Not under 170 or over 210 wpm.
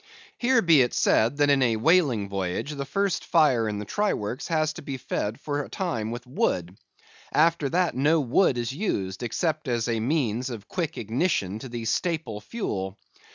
Yes: average, 190 wpm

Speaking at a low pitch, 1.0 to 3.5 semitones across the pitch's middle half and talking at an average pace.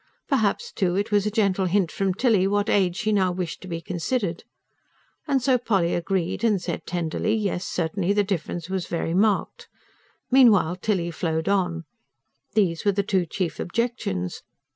No: high, 190 Hz; average, 3.2 semitones; average, 165 wpm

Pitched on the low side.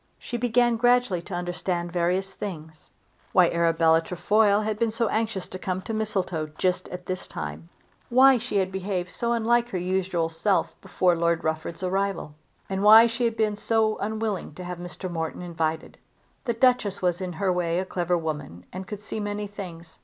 No: medium, 185 Hz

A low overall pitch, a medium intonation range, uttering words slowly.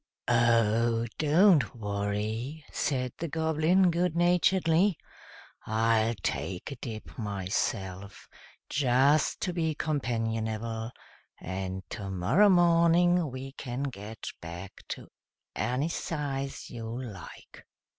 No: low, 125 Hz; wide, 6.6 semitones; slow, 95 wpm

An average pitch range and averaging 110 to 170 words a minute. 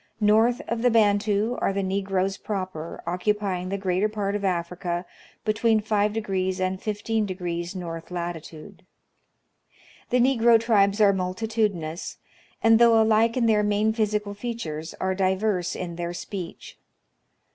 Yes: average, 3.1 semitones; slow, 135 wpm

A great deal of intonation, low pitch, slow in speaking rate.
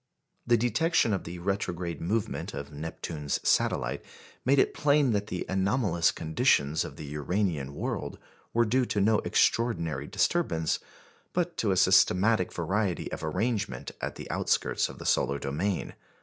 No: wide, 6.0 semitones; very low, 95 Hz; average, 150 wpm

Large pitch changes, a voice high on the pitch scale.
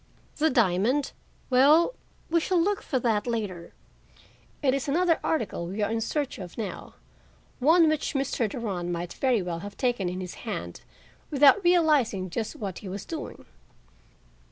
Yes: wide, 7.6 semitones; high, 240 Hz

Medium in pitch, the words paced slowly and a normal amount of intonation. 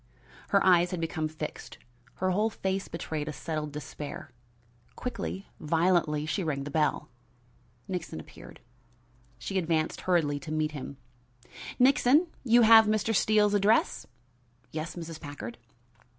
Yes: medium, 165 Hz; slow, 130 wpm; average, 4.7 semitones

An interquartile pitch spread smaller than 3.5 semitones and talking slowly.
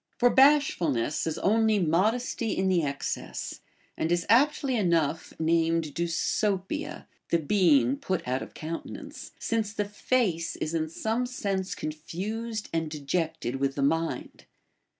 No: wide, 5.5 semitones; slow, 130 wpm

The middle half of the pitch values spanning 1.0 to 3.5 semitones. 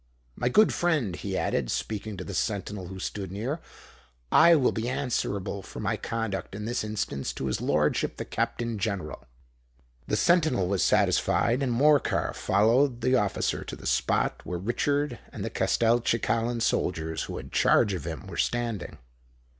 No: average, 4.2 semitones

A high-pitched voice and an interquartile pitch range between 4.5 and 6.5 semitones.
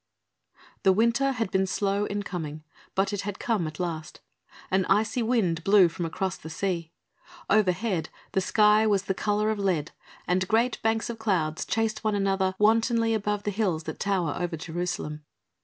No: high, 195 Hz; average, 3.5 semitones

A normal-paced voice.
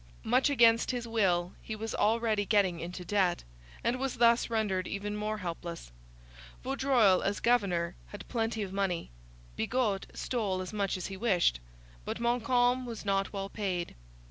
Yes: average, 155 wpm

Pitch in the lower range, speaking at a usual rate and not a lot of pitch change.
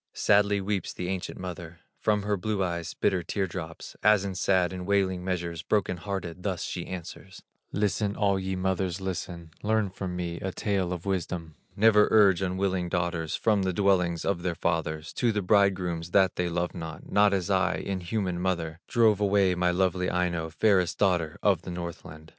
Yes: very low, 95 Hz; average, 180 wpm; narrow, 2.3 semitones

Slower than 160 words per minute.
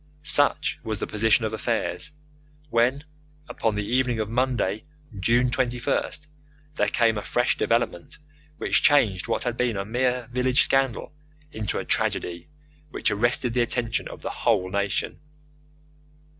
Yes: average, 145 wpm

